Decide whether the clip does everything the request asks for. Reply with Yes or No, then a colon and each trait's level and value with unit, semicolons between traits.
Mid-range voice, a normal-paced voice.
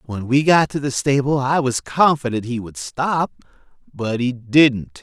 No: low, 130 Hz; average, 180 wpm